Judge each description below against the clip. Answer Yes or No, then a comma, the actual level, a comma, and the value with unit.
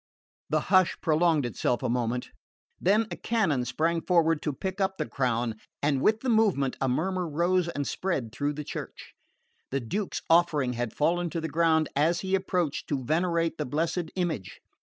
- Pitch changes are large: No, average, 4.6 semitones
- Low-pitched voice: No, medium, 160 Hz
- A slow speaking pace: No, average, 175 wpm